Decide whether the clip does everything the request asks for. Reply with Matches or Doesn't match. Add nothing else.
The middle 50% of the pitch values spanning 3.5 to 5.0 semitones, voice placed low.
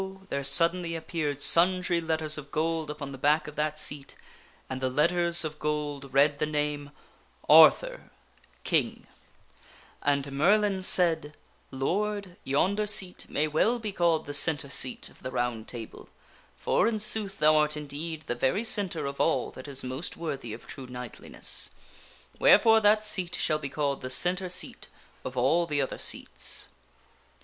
Doesn't match